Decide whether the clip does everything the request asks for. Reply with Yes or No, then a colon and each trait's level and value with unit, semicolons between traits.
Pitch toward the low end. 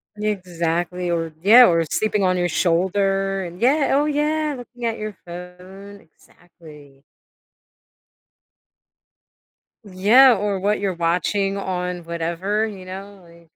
No: high, 190 Hz